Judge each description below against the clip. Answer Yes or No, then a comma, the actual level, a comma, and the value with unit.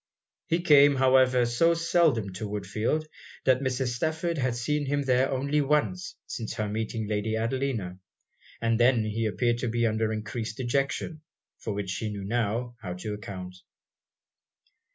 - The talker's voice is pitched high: No, low, 120 Hz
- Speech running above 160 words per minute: No, average, 155 wpm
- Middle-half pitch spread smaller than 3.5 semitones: No, average, 4.3 semitones